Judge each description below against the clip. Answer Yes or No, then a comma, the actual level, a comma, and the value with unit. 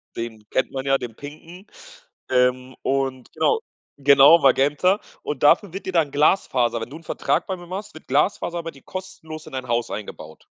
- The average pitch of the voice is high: No, medium, 140 Hz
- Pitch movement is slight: No, average, 4.8 semitones